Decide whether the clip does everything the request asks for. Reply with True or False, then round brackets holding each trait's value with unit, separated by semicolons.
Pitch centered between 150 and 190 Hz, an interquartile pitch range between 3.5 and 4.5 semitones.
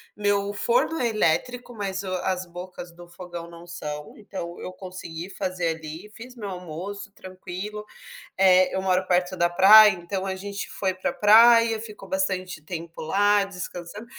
False (185 Hz; 2.8 semitones)